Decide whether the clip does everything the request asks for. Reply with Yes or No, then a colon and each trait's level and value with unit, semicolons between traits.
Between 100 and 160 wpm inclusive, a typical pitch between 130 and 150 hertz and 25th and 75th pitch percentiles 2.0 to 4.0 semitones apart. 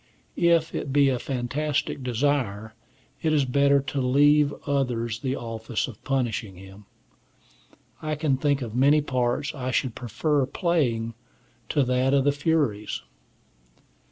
Yes: average, 140 wpm; low, 135 Hz; average, 3.3 semitones